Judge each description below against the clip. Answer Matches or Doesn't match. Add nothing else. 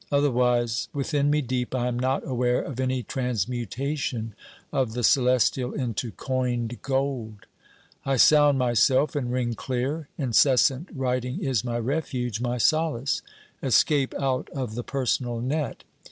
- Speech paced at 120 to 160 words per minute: Matches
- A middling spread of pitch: Doesn't match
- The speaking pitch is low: Matches